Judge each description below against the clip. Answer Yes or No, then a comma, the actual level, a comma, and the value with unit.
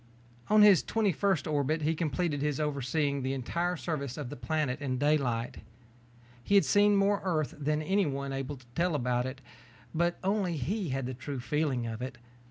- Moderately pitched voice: Yes, medium, 150 Hz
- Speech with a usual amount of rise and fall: Yes, average, 4.7 semitones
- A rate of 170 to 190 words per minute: Yes, average, 185 wpm